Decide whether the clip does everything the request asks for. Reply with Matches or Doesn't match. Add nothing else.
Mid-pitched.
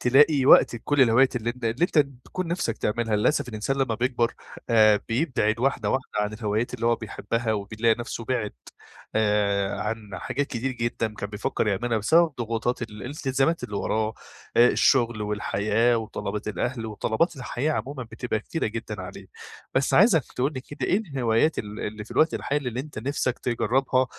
Doesn't match